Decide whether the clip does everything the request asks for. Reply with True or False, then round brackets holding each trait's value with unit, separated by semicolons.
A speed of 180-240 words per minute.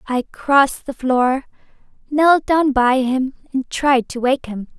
False (165 wpm)